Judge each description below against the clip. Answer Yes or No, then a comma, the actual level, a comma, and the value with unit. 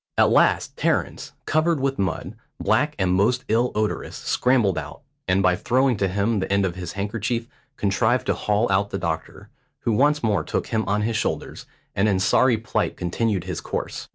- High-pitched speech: No, low, 105 Hz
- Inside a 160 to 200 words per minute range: Yes, average, 185 wpm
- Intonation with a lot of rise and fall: No, average, 4.0 semitones